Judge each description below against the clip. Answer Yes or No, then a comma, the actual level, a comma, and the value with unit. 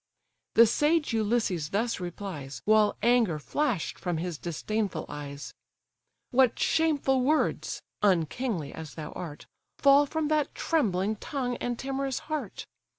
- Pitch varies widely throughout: Yes, wide, 7.6 semitones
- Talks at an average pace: No, slow, 125 wpm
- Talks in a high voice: Yes, high, 220 Hz